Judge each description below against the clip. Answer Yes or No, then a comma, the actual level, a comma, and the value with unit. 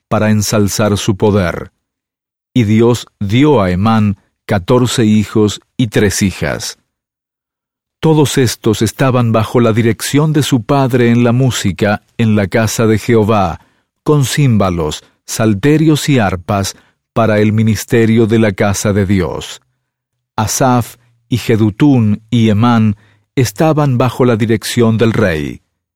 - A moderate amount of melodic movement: Yes, average, 3.0 semitones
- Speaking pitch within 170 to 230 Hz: No, low, 115 Hz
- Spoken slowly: Yes, slow, 130 wpm